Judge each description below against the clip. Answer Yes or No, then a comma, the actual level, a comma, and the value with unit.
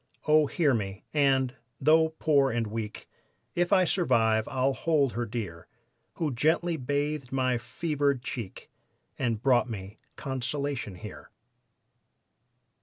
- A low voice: Yes, low, 130 Hz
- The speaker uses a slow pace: Yes, slow, 120 wpm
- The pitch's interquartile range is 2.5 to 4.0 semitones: No, average, 4.5 semitones